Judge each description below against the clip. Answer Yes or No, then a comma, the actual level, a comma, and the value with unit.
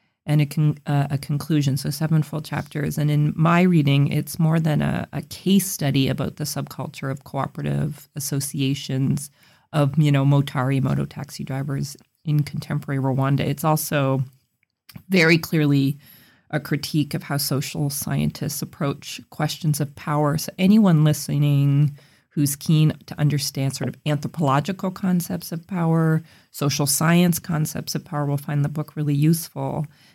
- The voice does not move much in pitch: Yes, narrow, 2.2 semitones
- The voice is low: No, medium, 150 Hz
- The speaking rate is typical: Yes, average, 150 wpm